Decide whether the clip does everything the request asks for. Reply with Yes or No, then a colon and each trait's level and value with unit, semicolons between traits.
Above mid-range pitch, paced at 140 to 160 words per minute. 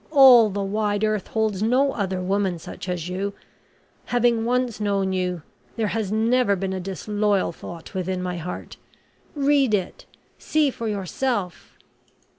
Yes: high, 205 Hz; average, 145 wpm